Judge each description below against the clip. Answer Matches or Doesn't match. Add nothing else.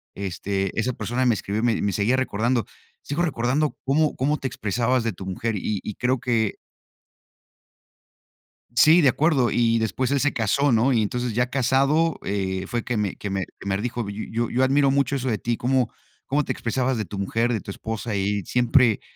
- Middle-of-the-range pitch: Doesn't match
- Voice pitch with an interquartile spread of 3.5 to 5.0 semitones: Matches